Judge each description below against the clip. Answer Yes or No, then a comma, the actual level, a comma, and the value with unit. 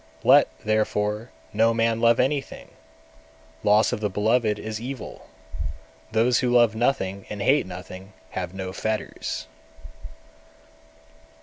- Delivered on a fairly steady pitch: Yes, narrow, 2.3 semitones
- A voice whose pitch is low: Yes, low, 110 Hz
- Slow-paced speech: Yes, slow, 120 wpm